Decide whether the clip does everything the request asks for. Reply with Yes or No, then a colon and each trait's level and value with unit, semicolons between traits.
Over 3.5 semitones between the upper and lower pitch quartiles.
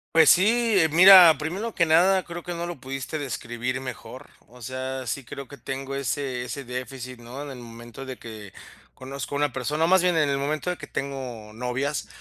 Yes: average, 4.4 semitones